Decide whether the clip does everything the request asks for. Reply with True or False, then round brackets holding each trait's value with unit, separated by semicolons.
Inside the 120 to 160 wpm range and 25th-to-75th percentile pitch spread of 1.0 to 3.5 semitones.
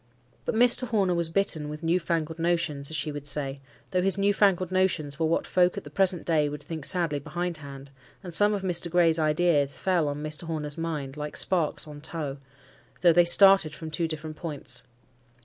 False (200 wpm; 3.1 semitones)